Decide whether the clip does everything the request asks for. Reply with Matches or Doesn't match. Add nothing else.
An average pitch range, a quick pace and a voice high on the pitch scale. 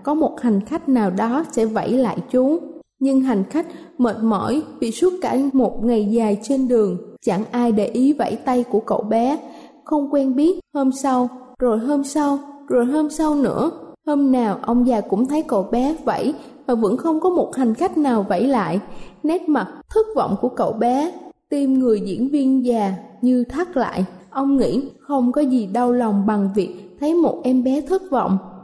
Doesn't match